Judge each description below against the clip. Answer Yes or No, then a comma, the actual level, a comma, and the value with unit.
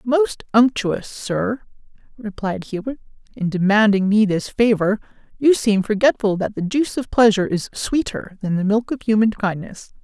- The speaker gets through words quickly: No, average, 155 wpm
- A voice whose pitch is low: No, high, 215 Hz